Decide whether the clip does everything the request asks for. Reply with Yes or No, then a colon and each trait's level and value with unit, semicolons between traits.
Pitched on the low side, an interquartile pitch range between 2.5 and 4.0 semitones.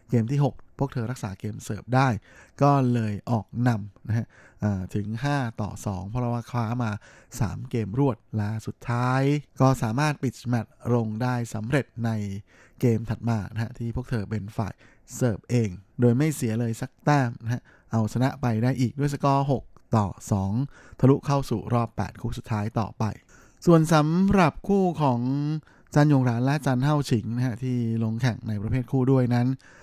Yes: low, 120 Hz; average, 3.2 semitones